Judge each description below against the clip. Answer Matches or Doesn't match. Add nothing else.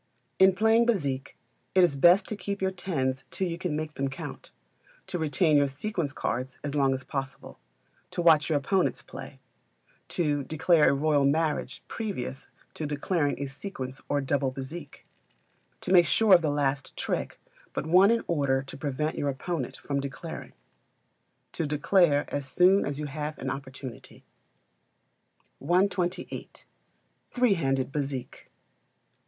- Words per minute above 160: Doesn't match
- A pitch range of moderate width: Matches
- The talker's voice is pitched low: Doesn't match